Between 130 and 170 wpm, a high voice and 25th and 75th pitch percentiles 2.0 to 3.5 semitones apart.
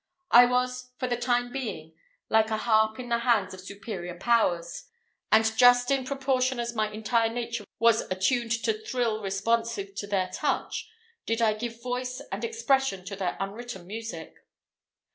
Yes: average, 160 wpm; high, 230 Hz; average, 3.1 semitones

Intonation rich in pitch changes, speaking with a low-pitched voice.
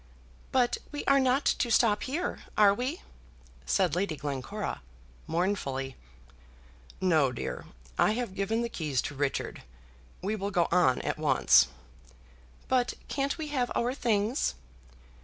No: wide, 7.1 semitones; high, 205 Hz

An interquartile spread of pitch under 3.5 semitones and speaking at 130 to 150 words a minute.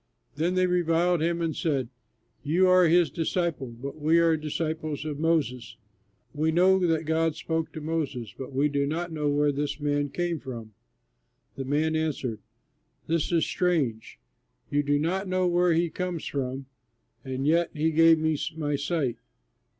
No: average, 2.8 semitones; average, 165 wpm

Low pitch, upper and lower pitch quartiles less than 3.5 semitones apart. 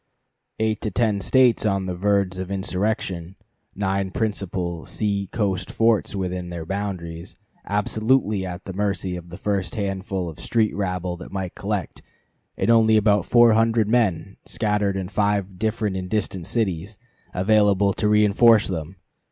Yes: low, 100 Hz; narrow, 2.6 semitones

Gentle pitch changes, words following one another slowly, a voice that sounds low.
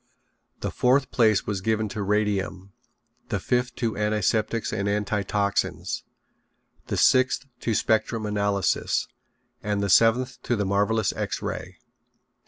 Yes: narrow, 2.2 semitones; slow, 125 wpm; low, 105 Hz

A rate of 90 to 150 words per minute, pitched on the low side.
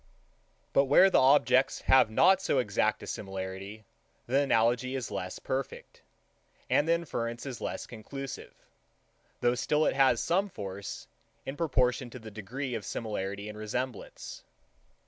Yes: average, 145 wpm; low, 125 Hz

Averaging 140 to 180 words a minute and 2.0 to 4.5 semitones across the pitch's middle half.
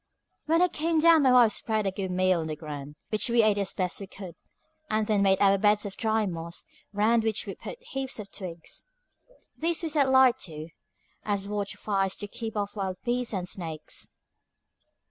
No: average, 200 wpm; average, 4.1 semitones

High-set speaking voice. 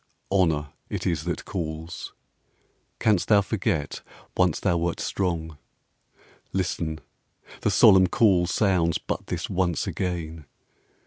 No: very low, 85 Hz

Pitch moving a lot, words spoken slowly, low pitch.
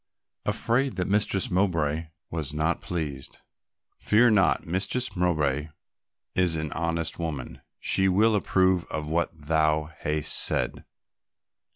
No: average, 3.7 semitones; slow, 115 wpm; very low, 85 Hz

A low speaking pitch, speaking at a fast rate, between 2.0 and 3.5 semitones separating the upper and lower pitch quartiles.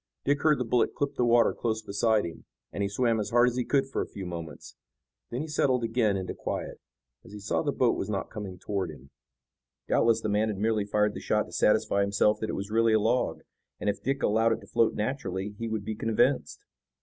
Yes: low, 110 Hz; fast, 235 wpm; average, 2.8 semitones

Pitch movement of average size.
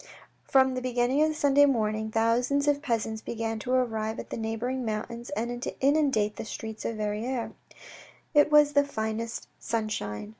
Yes: average, 3.6 semitones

